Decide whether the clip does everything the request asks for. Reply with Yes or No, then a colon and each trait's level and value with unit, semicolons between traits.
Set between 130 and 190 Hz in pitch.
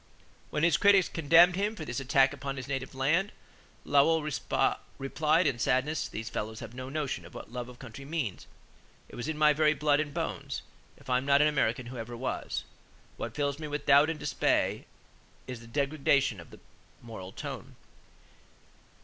Yes: medium, 140 Hz